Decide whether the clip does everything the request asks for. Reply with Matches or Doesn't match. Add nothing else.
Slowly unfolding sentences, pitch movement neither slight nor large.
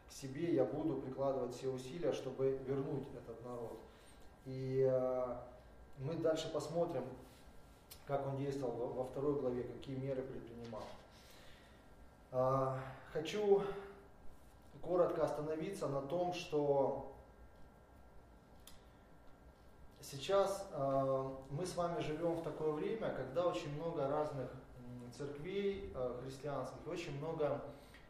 Matches